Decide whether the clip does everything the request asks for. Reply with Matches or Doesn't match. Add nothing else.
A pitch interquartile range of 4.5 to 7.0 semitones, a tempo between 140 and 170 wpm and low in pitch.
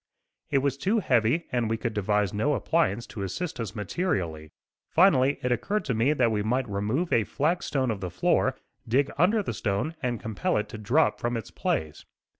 Doesn't match